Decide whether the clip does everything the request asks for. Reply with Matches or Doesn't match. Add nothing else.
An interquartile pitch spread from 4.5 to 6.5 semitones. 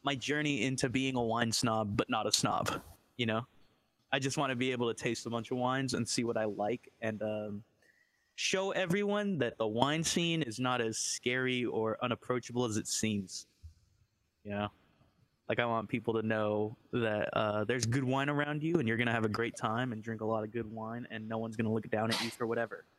Doesn't match